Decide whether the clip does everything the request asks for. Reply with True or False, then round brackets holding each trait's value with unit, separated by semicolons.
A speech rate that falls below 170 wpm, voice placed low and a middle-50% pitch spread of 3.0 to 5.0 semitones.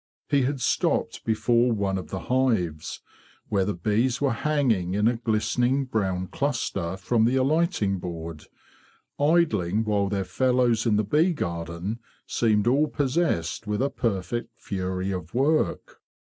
False (145 wpm; 110 Hz; 5.5 semitones)